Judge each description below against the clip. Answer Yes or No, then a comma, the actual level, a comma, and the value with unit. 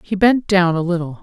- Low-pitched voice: No, medium, 185 Hz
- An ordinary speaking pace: No, fast, 245 wpm